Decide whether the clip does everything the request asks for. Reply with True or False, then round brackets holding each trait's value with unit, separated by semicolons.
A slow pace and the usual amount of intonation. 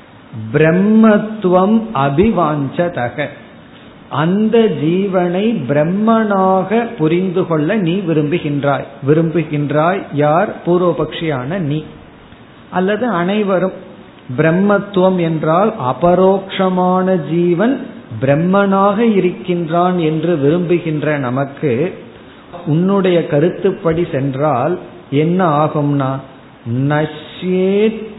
True (60 wpm; 4.1 semitones)